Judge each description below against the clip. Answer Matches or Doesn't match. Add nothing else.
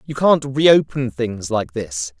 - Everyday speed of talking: Matches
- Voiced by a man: Matches